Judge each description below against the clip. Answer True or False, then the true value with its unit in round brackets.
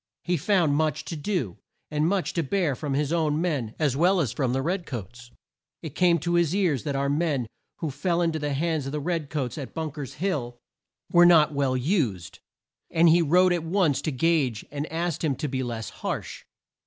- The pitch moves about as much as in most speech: True (3.9 semitones)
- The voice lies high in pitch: False (155 Hz)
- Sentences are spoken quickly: True (215 wpm)